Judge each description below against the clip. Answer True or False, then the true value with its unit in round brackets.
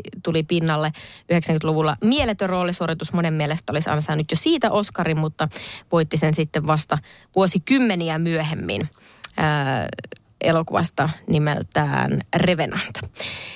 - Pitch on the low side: False (160 Hz)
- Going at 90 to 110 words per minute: True (100 wpm)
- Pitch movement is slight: True (2.2 semitones)